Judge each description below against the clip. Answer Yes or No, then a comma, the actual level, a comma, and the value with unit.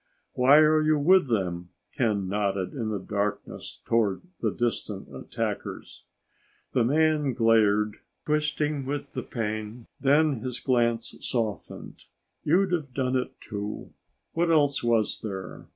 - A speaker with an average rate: No, slow, 130 wpm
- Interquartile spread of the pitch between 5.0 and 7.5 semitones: Yes, wide, 5.6 semitones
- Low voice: Yes, low, 120 Hz